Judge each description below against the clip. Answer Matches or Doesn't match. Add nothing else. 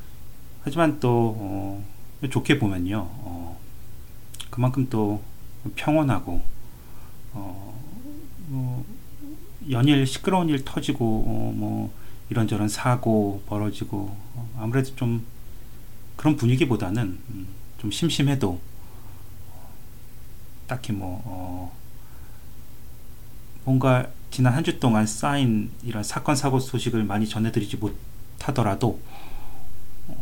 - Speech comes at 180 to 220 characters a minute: Matches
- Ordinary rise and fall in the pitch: Matches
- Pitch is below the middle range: Matches